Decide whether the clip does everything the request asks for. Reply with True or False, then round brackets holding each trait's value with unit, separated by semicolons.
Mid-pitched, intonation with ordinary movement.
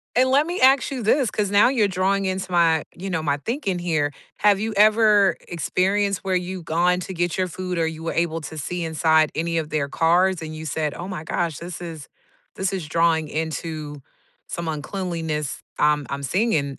True (175 Hz; 3.5 semitones)